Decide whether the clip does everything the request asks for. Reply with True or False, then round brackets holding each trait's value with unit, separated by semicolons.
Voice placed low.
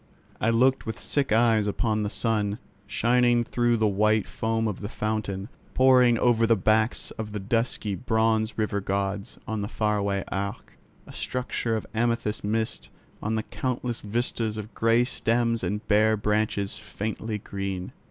True (110 Hz)